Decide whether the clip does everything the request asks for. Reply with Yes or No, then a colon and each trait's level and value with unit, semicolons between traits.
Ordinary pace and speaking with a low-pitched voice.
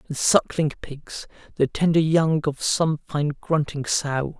No: average, 150 wpm; medium, 150 Hz